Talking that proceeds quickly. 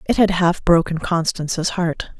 No: average, 165 wpm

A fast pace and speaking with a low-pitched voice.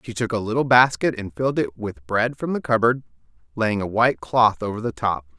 Yes: fast, 225 wpm; low, 110 Hz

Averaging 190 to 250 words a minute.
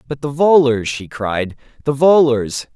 No: average, 150 wpm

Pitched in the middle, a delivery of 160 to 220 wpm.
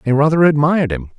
Yes: medium, 145 Hz; average, 200 wpm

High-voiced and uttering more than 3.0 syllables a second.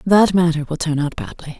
No: medium, 160 Hz; 5.5 syllables/s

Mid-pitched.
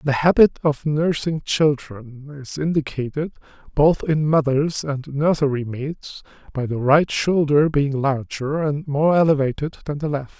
Yes: medium, 145 Hz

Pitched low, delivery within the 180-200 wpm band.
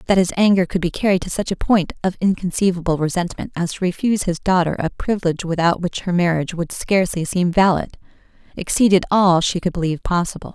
No: medium, 180 Hz; average, 195 wpm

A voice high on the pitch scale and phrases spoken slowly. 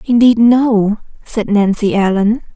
Yes: high, 220 Hz; slow, 115 wpm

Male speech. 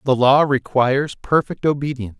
Yes: male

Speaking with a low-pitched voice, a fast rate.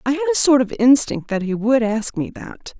No: very high, 250 Hz; fast, 260 wpm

